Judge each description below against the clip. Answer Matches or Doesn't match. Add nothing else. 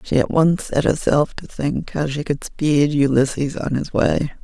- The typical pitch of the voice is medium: Matches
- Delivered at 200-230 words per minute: Matches